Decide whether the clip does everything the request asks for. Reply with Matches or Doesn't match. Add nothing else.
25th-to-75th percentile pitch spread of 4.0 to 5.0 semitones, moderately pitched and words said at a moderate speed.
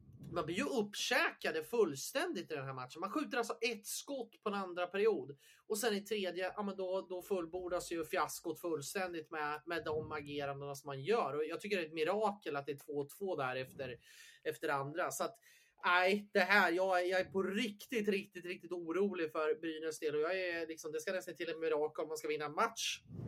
Doesn't match